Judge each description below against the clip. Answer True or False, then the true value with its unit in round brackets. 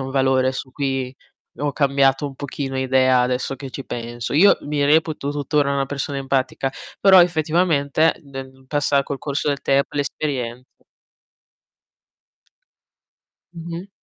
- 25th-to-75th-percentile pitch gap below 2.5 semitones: True (1.8 semitones)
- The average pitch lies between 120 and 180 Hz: True (140 Hz)